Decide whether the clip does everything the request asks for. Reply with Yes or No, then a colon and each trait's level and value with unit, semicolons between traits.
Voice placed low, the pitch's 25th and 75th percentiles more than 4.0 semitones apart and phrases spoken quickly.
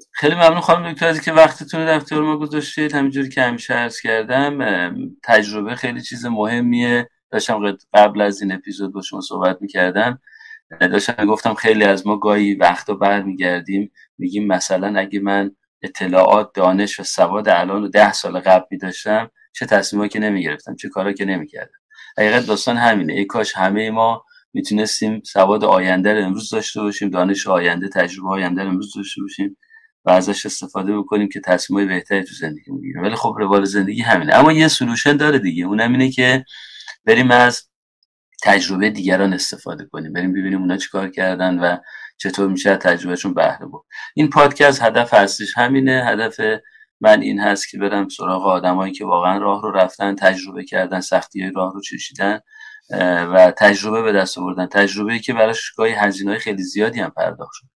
Yes: low, 105 Hz; average, 5.2 semitones; fast, 170 wpm